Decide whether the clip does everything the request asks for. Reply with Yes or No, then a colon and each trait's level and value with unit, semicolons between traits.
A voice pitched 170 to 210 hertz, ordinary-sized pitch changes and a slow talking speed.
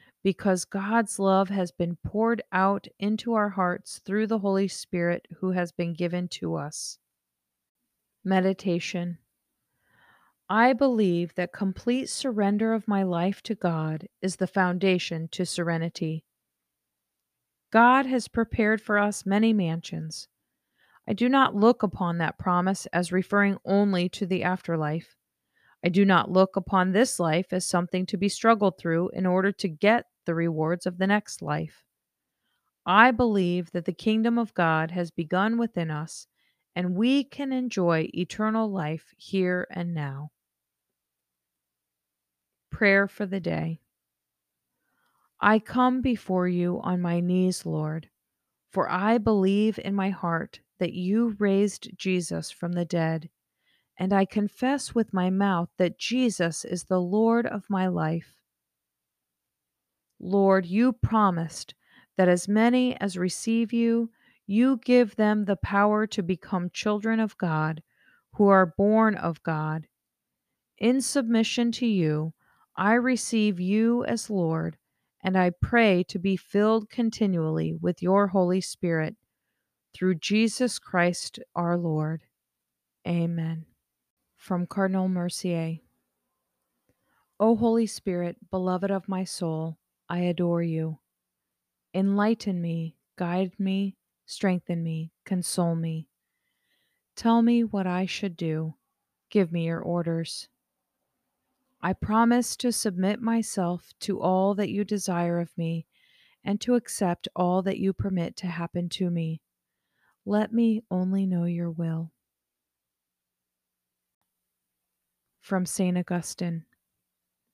Yes: medium, 185 Hz; average, 4.0 semitones; slow, 130 wpm